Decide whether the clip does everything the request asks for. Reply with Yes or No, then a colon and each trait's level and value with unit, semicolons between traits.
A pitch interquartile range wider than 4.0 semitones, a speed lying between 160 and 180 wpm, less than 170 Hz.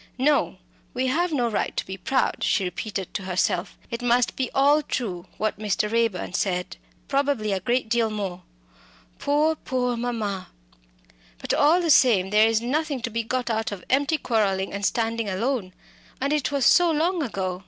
No: average, 5.3 semitones; average, 175 wpm; high, 230 Hz